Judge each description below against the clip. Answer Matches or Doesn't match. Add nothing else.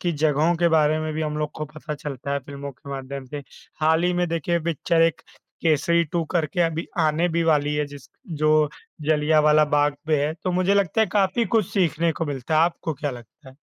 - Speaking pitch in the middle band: Matches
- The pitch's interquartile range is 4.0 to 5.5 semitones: Doesn't match